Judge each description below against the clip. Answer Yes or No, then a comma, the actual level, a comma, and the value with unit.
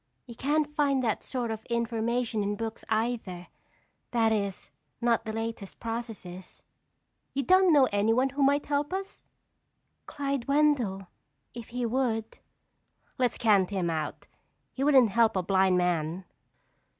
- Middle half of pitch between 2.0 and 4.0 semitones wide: No, average, 4.8 semitones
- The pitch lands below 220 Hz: No, high, 230 Hz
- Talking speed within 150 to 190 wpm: No, slow, 135 wpm